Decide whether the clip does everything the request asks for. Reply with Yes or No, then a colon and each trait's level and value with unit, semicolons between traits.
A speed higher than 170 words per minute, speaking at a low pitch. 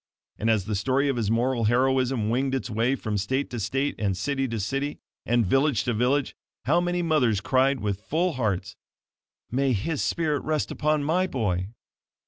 Yes: average, 180 wpm; low, 130 Hz